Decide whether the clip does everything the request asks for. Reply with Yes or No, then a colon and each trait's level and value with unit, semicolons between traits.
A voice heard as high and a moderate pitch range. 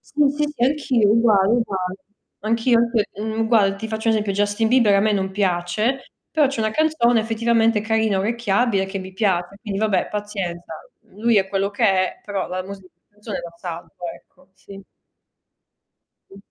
Yes: high, 210 Hz; average, 3.0 semitones